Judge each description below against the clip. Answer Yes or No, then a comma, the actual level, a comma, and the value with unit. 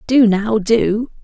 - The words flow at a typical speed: Yes, average, 145 wpm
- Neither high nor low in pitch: No, high, 220 Hz